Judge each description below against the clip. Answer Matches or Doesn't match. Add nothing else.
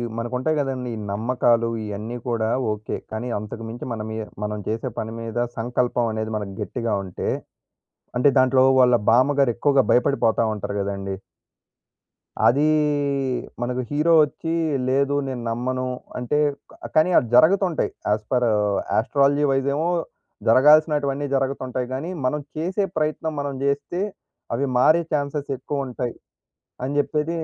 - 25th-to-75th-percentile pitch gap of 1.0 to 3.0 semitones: Doesn't match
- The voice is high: Doesn't match